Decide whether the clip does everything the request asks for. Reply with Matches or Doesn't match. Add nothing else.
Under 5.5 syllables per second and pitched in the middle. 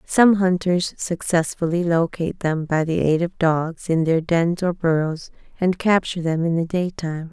Matches